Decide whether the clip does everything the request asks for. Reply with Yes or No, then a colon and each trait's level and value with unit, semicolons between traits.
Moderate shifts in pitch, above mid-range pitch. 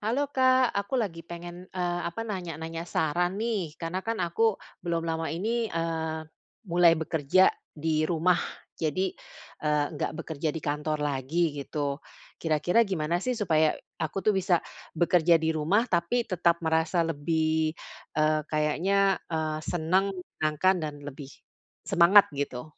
No: average, 3.1 semitones; medium, 165 Hz